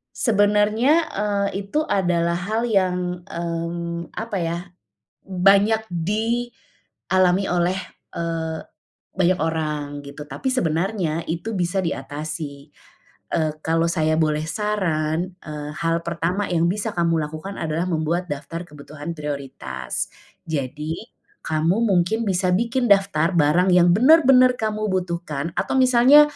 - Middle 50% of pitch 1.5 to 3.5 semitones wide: No, average, 4.1 semitones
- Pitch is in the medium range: Yes, medium, 175 Hz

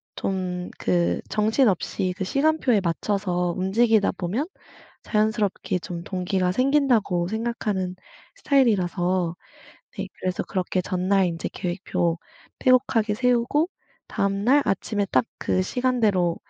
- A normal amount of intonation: Yes, average, 4.5 semitones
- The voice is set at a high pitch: Yes, high, 195 Hz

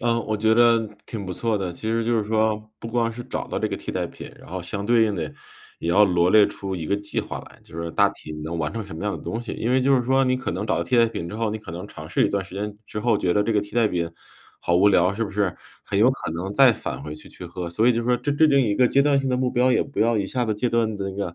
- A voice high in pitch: No, low, 105 Hz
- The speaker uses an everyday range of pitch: Yes, average, 3.8 semitones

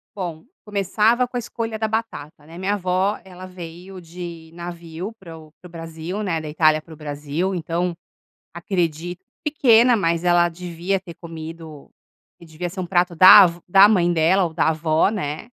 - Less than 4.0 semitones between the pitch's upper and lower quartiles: Yes, average, 2.9 semitones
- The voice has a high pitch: No, medium, 175 Hz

